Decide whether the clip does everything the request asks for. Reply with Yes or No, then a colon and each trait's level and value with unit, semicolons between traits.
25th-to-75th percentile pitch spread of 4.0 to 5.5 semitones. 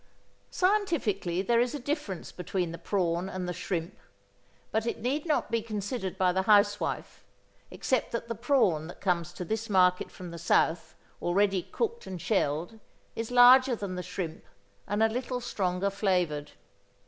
Yes: average, 4.7 semitones